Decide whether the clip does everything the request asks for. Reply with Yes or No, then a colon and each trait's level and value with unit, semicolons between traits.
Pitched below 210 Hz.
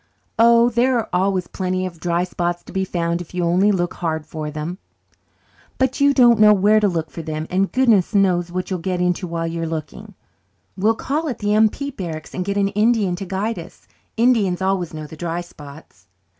Yes: medium, 185 Hz